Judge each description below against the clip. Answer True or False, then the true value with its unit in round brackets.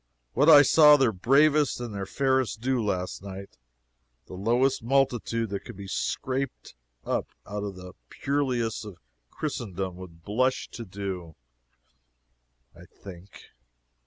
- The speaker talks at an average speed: False (130 wpm)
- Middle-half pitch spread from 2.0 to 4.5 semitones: False (5.6 semitones)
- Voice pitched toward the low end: True (115 Hz)